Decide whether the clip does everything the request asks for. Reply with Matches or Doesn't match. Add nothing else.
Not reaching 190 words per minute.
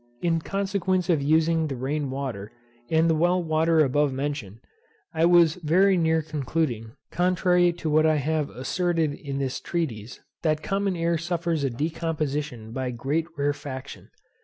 Matches